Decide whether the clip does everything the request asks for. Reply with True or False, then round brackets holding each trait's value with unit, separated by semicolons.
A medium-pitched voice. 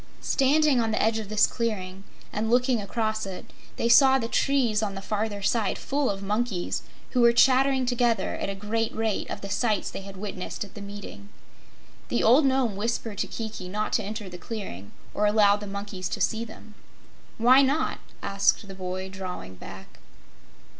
False (215 Hz)